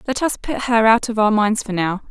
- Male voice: No, female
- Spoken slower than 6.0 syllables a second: Yes, 5.3 syllables/s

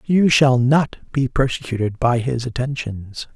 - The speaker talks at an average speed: Yes, average, 145 wpm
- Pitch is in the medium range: No, low, 125 Hz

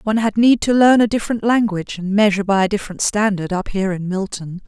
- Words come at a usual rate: No, fast, 230 wpm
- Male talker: No, female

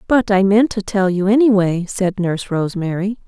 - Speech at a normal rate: Yes, average, 185 wpm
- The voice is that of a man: No, female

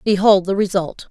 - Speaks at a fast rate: No, average, 165 wpm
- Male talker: No, female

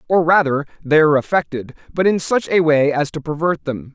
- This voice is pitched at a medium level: Yes, medium, 155 Hz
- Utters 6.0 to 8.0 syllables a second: No, 5.5 syllables/s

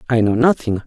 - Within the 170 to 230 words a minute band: Yes, fast, 205 wpm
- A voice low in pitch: Yes, low, 120 Hz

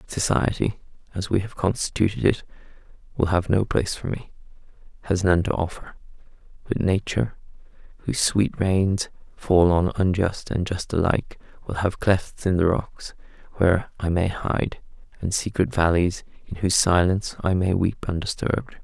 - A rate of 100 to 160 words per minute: Yes, average, 150 wpm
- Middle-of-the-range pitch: No, very low, 95 Hz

